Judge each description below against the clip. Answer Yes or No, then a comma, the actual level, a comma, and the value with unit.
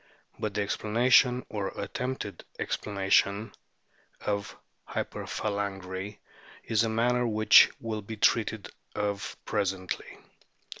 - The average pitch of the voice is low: Yes, low, 105 Hz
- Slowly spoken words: Yes, slow, 95 wpm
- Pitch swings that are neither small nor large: No, narrow, 2.1 semitones